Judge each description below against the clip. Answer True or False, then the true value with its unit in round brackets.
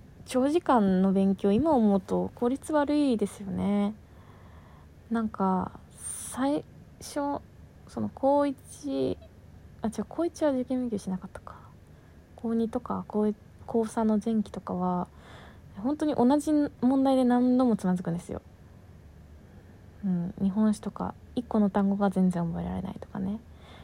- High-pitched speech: True (205 Hz)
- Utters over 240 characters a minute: False (235 characters per minute)